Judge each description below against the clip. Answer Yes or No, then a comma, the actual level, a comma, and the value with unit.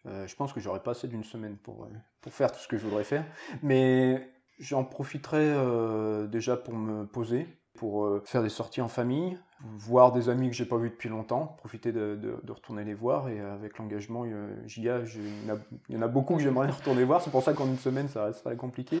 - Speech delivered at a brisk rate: Yes, fast, 235 wpm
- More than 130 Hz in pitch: No, low, 120 Hz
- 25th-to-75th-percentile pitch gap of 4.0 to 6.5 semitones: No, average, 3.2 semitones